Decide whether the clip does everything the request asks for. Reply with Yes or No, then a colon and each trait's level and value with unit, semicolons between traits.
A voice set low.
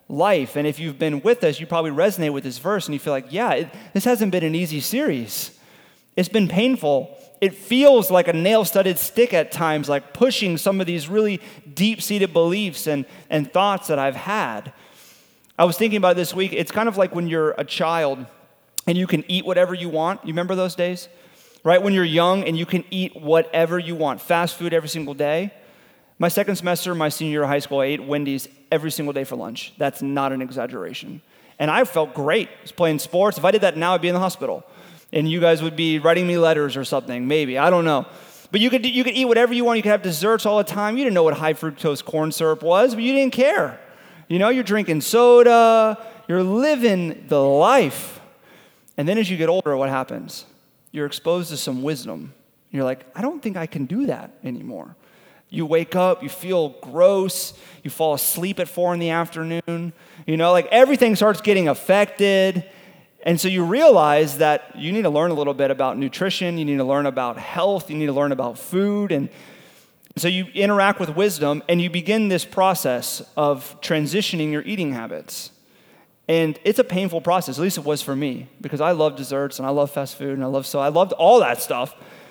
No: medium, 170 Hz